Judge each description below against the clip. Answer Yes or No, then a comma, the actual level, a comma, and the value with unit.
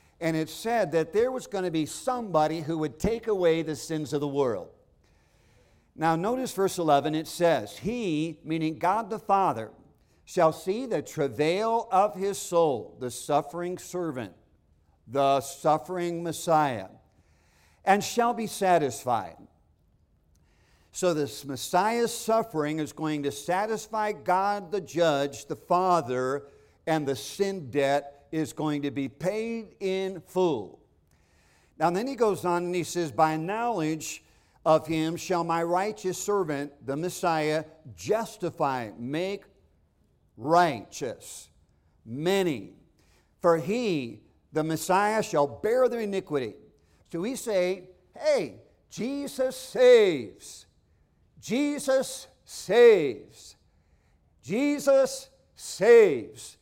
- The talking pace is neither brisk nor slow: No, slow, 120 wpm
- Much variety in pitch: Yes, wide, 6.3 semitones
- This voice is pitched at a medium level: Yes, medium, 165 Hz